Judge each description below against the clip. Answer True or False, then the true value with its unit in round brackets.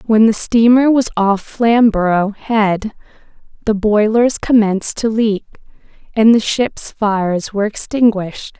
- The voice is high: True (215 Hz)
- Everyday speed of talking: False (125 wpm)